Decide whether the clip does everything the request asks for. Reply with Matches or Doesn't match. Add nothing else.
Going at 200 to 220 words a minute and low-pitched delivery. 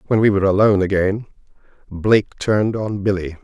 Doesn't match